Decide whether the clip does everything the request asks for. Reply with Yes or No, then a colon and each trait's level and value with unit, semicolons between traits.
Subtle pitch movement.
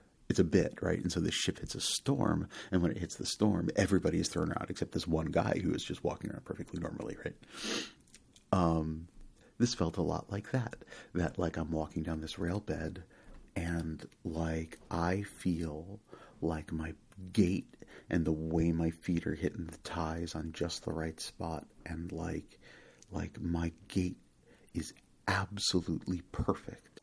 Yes: narrow, 2.1 semitones